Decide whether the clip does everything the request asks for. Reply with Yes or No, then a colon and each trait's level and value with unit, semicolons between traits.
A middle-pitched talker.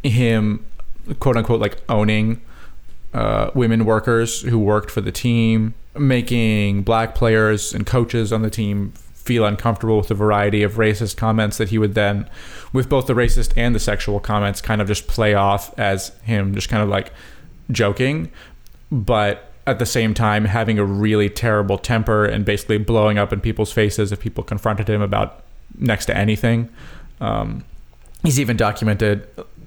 No: low, 110 Hz